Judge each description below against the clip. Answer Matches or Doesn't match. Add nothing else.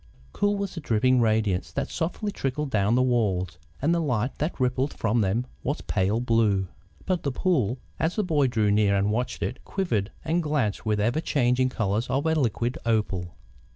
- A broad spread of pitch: Matches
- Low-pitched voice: Matches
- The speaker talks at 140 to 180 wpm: Doesn't match